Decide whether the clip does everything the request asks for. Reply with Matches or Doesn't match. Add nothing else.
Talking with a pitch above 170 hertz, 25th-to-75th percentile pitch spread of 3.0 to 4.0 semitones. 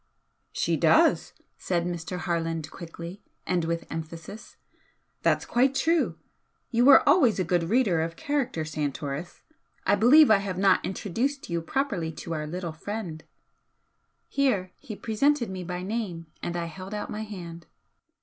Doesn't match